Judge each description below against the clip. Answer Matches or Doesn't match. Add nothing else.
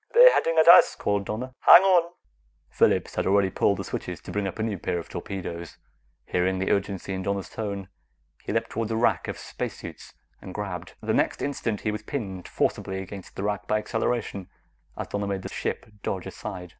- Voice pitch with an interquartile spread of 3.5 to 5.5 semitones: Doesn't match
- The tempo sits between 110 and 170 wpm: Doesn't match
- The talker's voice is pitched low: Matches